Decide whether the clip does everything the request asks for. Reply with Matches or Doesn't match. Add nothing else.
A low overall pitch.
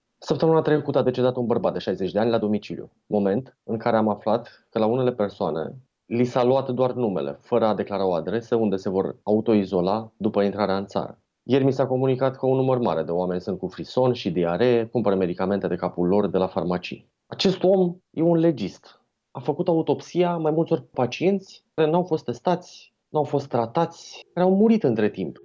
Matches